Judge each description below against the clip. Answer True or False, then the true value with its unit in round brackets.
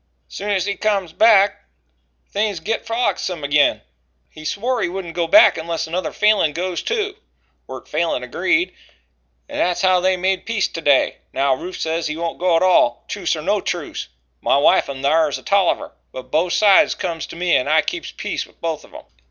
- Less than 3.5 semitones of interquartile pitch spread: False (4.0 semitones)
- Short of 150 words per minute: False (195 wpm)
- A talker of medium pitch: True (180 Hz)